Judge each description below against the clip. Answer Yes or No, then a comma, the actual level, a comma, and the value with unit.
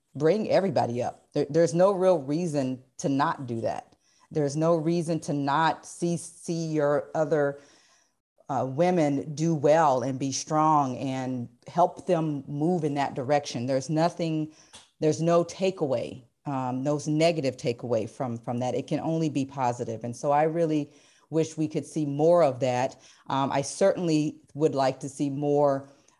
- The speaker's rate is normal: Yes, average, 165 wpm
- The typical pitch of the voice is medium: Yes, medium, 150 Hz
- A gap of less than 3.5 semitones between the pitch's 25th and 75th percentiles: Yes, average, 2.9 semitones